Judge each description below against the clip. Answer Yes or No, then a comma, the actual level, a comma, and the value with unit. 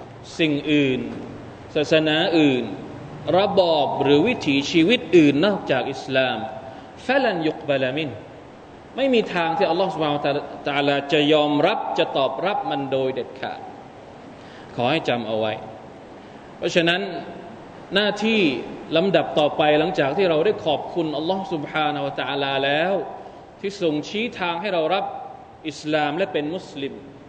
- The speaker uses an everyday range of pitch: Yes, average, 3.7 semitones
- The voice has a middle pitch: Yes, medium, 155 Hz